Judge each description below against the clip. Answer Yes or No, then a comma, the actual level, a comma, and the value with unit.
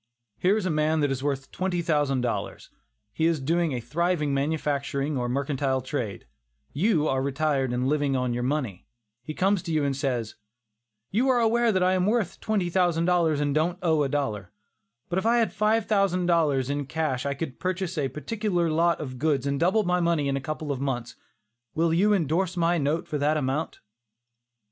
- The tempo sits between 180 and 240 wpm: Yes, average, 195 wpm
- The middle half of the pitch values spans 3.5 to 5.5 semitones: Yes, average, 4.4 semitones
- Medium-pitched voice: Yes, medium, 155 Hz